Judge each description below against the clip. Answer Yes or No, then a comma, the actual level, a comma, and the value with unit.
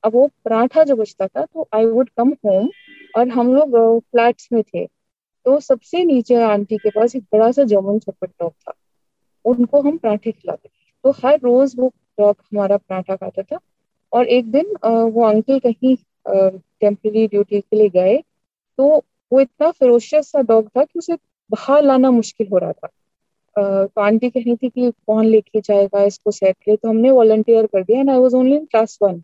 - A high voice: Yes, high, 230 Hz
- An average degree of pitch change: Yes, average, 4.0 semitones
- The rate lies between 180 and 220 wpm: Yes, average, 185 wpm